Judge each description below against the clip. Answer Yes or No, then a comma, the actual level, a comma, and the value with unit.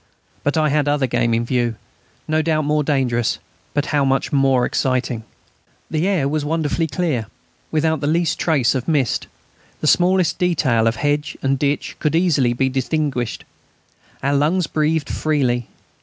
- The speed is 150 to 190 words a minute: Yes, average, 155 wpm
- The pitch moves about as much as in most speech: Yes, average, 3.5 semitones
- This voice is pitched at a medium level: Yes, medium, 145 Hz